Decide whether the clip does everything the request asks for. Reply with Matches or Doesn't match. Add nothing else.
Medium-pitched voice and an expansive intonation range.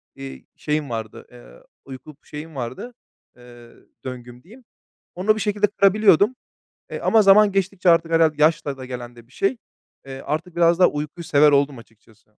Matches